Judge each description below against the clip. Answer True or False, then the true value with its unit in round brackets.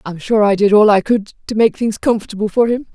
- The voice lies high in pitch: True (215 Hz)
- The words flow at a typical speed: False (265 wpm)